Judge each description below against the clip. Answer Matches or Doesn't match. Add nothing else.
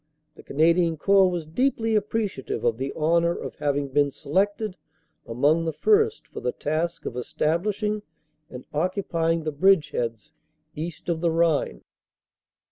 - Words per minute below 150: Matches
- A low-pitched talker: Doesn't match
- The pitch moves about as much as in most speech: Matches